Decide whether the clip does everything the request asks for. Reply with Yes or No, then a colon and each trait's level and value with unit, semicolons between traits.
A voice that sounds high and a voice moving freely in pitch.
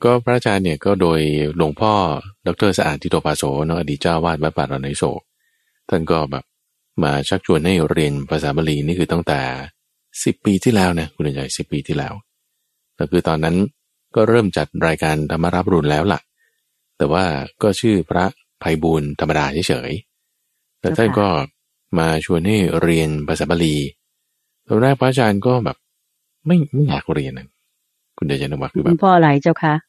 No: very low, 85 Hz; wide, 6.1 semitones